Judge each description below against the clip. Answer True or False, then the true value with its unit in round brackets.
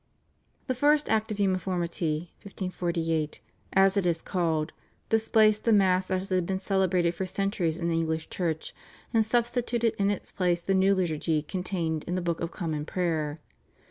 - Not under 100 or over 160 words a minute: False (170 wpm)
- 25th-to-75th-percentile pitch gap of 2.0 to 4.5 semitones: True (3.1 semitones)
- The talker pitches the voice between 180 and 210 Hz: True (185 Hz)